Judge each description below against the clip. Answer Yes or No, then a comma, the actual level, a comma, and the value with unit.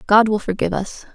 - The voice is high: Yes, high, 205 Hz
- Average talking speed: No, fast, 210 wpm